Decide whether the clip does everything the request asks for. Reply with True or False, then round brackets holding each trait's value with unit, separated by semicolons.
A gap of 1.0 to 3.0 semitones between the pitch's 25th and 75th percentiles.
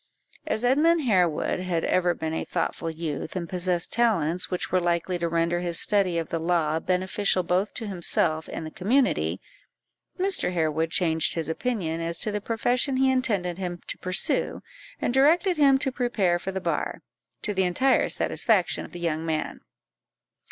False (5.1 semitones)